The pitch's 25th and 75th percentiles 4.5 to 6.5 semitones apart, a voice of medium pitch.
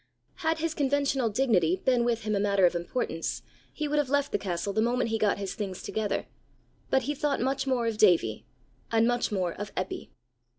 No: average, 5.2 semitones; high, 225 Hz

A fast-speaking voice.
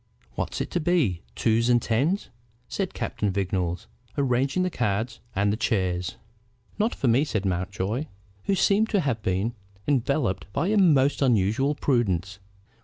No: average, 150 wpm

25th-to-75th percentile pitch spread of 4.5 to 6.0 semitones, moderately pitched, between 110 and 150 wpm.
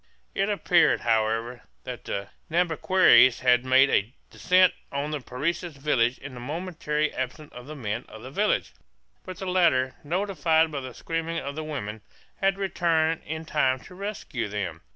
No: wide, 5.5 semitones; medium, 150 Hz; average, 165 wpm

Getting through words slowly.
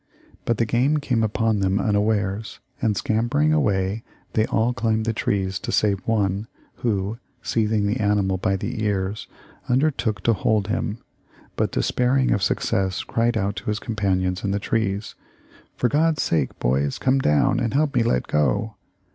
No: average, 160 wpm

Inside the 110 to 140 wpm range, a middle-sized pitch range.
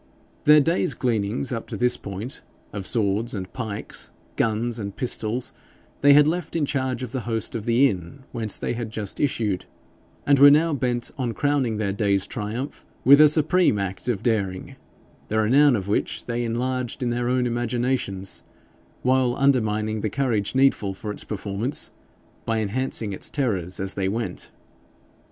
No: average, 165 wpm; average, 3.9 semitones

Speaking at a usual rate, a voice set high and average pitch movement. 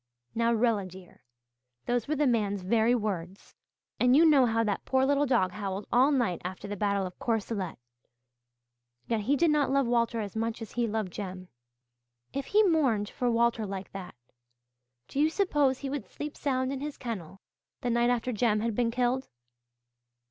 Yes: average, 180 wpm; high, 235 Hz; average, 4.4 semitones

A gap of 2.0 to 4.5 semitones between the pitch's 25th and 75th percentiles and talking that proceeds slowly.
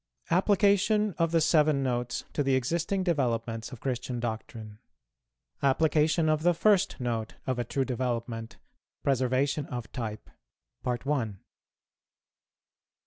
No: wide, 5.5 semitones; slow, 110 wpm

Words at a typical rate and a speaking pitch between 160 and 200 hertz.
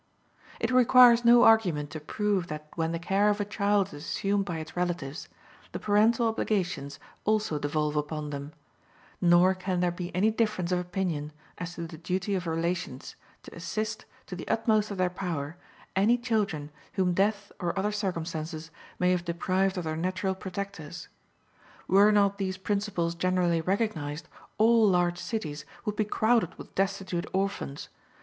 Yes: average, 160 wpm; medium, 185 Hz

